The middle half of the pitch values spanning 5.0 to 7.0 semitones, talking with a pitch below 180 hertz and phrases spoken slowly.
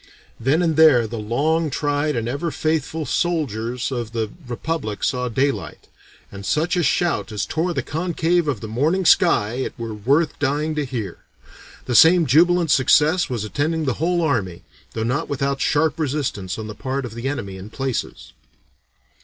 No: wide, 5.6 semitones; medium, 140 Hz; average, 170 wpm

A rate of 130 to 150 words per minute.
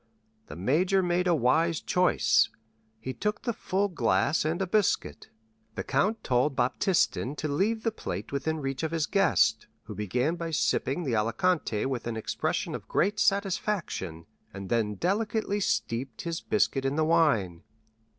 No: average, 160 wpm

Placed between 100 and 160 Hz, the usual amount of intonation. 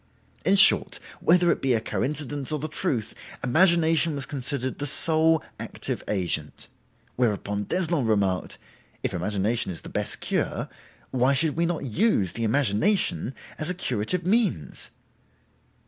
No: medium, 140 Hz; wide, 7.0 semitones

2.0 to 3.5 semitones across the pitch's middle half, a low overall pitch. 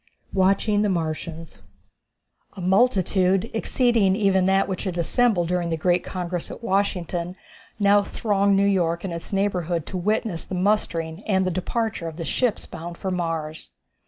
No: average, 2.8 semitones; medium, 185 Hz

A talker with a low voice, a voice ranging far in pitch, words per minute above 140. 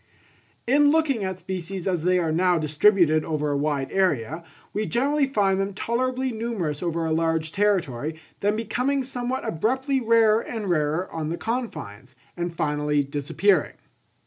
No: medium, 185 Hz; wide, 6.6 semitones; average, 150 wpm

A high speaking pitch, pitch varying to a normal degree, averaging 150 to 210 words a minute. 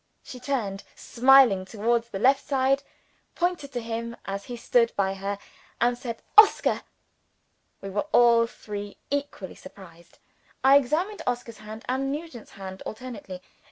No: high, 235 Hz; average, 4.9 semitones; average, 140 wpm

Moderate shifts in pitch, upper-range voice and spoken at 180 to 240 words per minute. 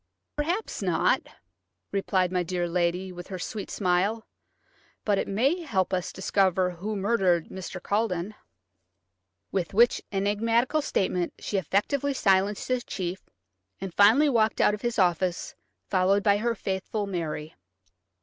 No: average, 3.3 semitones; high, 195 Hz; average, 140 wpm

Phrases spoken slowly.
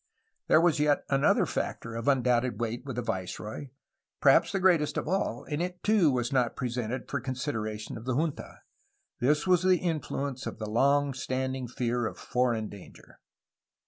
No: average, 175 wpm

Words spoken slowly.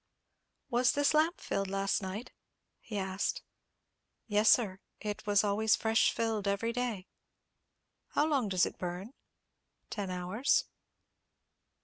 Yes: slow, 120 wpm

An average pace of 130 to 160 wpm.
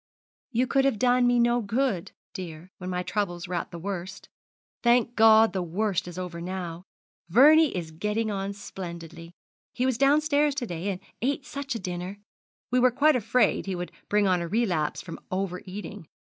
No: average, 185 wpm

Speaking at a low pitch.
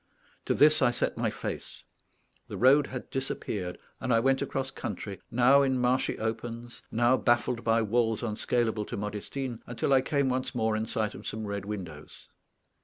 Yes: low, 120 Hz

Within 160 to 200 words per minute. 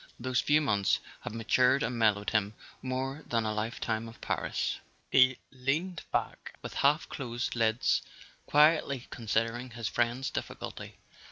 No: average, 145 wpm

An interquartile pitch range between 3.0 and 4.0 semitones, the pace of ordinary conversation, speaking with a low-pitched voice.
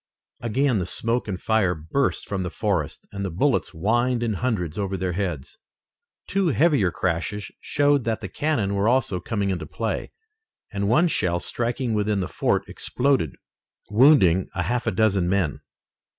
No: average, 5.0 semitones; average, 160 wpm; low, 105 Hz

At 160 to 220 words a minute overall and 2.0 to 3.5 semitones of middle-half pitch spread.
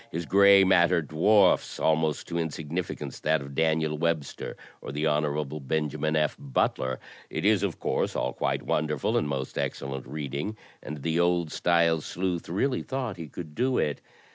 Yes: average, 170 wpm; average, 2.8 semitones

